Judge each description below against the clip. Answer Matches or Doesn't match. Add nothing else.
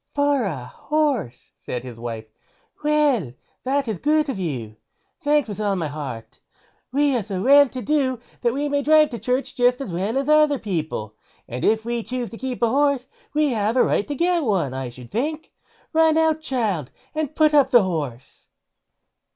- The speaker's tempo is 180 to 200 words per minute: Matches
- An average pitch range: Doesn't match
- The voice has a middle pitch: Doesn't match